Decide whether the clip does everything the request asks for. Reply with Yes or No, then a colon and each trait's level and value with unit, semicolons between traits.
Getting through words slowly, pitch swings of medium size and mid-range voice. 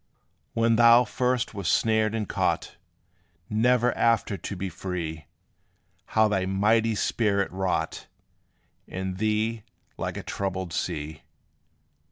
No: slow, 115 wpm; average, 3.4 semitones; low, 105 Hz